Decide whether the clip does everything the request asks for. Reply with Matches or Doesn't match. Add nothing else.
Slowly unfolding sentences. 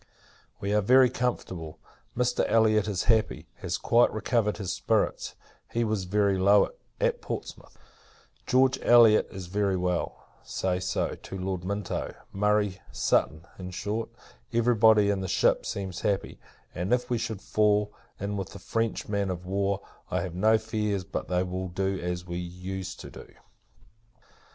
Doesn't match